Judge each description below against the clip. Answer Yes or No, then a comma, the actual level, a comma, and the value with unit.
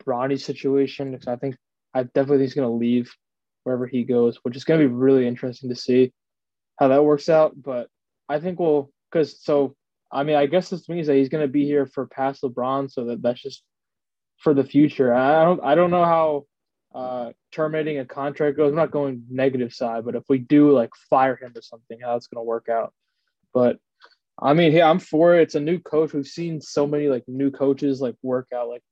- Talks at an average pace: No, fast, 220 wpm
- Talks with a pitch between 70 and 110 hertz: No, low, 135 Hz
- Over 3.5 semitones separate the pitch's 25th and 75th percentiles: No, average, 2.9 semitones